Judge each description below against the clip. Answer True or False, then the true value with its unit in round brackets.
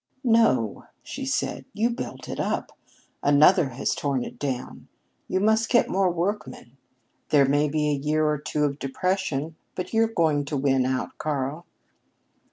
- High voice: False (150 Hz)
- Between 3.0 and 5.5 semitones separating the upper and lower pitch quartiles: True (5.2 semitones)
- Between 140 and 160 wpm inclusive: True (150 wpm)